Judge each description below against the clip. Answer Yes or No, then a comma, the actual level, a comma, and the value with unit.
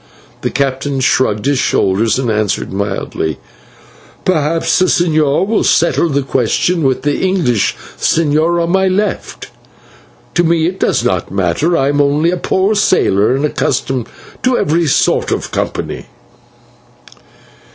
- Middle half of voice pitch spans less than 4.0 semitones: No, average, 5.0 semitones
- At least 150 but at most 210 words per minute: No, average, 140 wpm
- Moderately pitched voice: Yes, medium, 145 Hz